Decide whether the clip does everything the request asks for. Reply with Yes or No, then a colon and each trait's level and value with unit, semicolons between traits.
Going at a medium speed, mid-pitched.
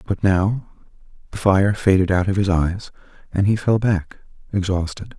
No: average, 160 wpm; very low, 95 Hz